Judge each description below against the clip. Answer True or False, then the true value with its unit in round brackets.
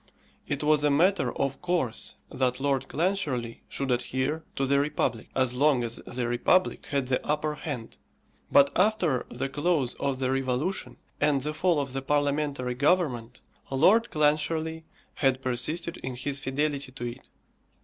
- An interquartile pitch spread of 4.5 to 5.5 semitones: False (3.0 semitones)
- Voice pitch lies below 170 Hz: True (140 Hz)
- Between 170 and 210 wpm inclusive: False (155 wpm)